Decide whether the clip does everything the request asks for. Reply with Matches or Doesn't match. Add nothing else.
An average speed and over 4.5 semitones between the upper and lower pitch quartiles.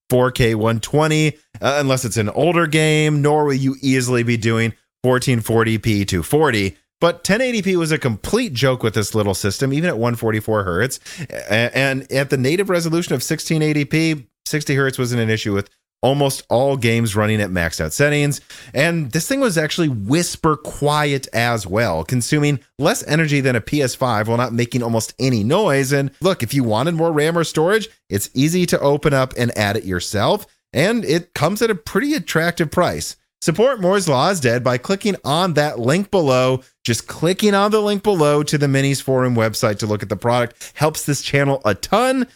Matches